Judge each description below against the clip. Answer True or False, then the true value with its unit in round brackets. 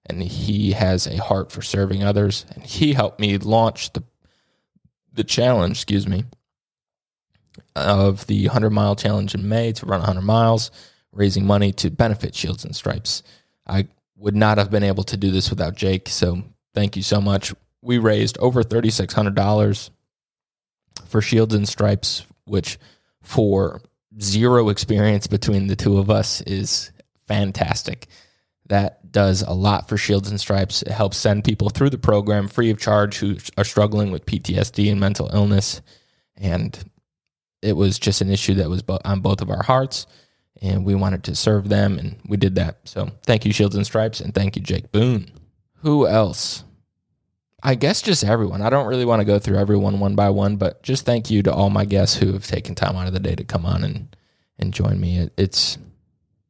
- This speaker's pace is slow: False (185 wpm)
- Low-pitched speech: True (100 Hz)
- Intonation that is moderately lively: False (1.8 semitones)